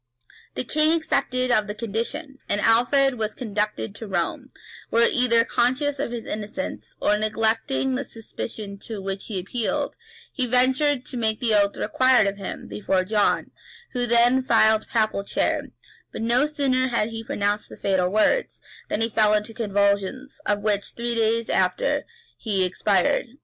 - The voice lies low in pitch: No, high, 225 Hz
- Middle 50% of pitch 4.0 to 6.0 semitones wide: No, average, 3.3 semitones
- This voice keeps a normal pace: Yes, average, 165 wpm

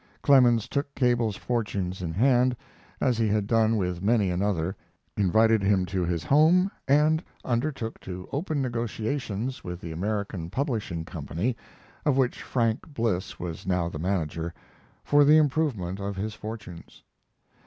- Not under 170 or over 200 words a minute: No, average, 145 wpm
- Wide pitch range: Yes, wide, 5.8 semitones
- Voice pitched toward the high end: No, low, 110 Hz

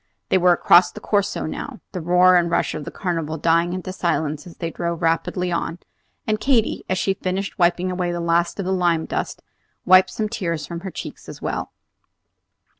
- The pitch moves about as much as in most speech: No, narrow, 1.7 semitones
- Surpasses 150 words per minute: Yes, average, 195 wpm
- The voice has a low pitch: No, medium, 175 Hz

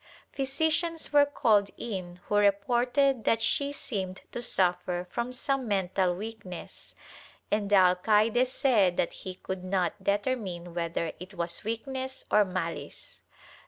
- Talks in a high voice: Yes, high, 205 Hz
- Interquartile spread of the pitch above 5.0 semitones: Yes, wide, 5.4 semitones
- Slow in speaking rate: Yes, slow, 130 wpm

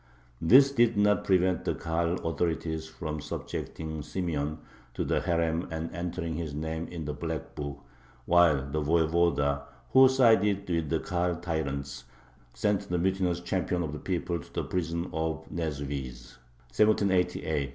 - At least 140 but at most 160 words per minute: Yes, average, 145 wpm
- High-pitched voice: No, very low, 85 Hz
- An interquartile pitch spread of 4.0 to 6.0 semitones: No, average, 2.7 semitones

